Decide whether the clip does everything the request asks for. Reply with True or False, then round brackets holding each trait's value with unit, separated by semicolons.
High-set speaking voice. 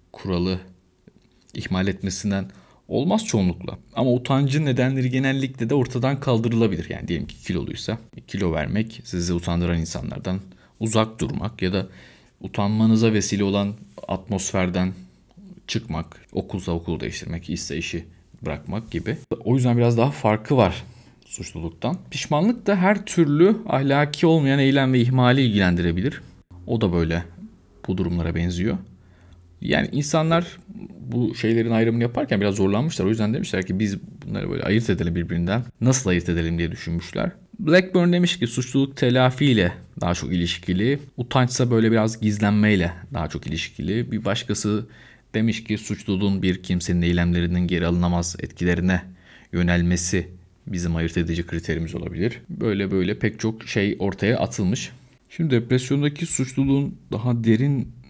False (105 Hz)